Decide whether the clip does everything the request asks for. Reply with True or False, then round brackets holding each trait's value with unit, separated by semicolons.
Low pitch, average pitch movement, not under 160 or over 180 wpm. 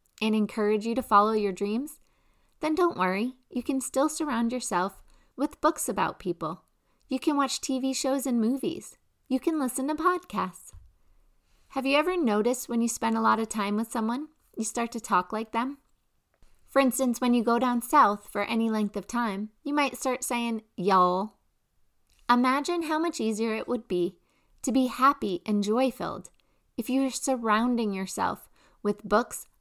False (240 Hz; 4.0 semitones; 175 wpm)